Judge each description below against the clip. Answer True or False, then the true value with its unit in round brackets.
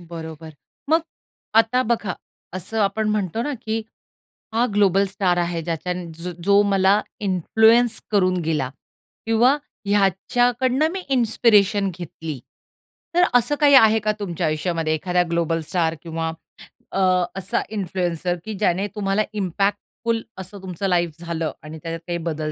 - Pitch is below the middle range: False (190 Hz)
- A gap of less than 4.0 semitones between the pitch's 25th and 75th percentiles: False (4.4 semitones)